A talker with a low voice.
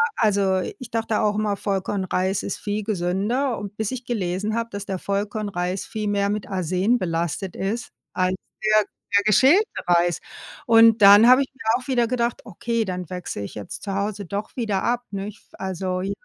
No: high, 205 Hz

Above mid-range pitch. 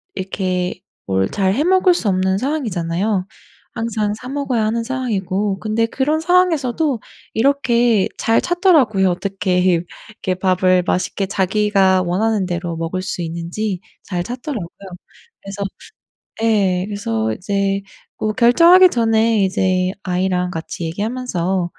Yes: high, 200 Hz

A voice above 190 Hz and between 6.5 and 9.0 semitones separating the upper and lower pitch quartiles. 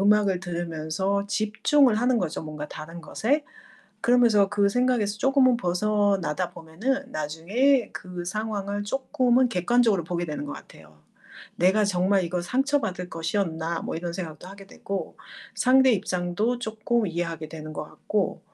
No: high, 200 Hz; average, 5.3 semitones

